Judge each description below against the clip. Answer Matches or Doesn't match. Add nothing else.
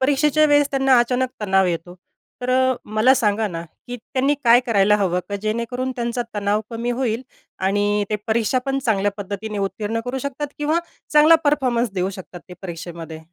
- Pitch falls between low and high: Doesn't match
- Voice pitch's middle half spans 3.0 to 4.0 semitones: Doesn't match